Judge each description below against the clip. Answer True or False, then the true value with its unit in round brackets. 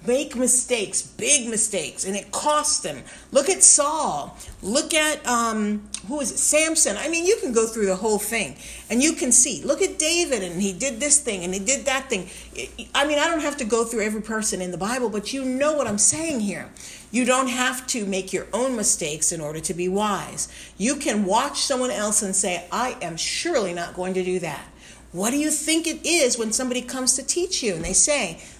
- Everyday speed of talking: False (225 wpm)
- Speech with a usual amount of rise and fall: False (6.3 semitones)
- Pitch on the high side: True (245 Hz)